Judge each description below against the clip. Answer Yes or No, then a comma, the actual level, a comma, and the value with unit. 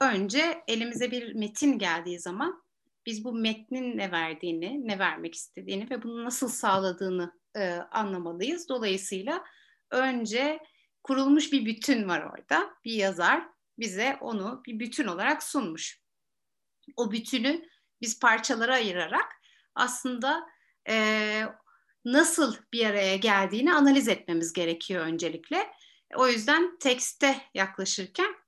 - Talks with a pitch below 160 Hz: No, high, 235 Hz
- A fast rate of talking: No, average, 115 wpm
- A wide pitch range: Yes, wide, 6.2 semitones